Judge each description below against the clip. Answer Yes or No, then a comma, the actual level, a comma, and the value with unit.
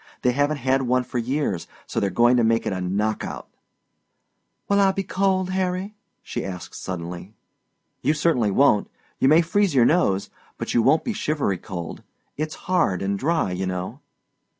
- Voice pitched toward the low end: Yes, low, 125 Hz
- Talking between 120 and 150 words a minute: No, average, 175 wpm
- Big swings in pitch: Yes, wide, 8.8 semitones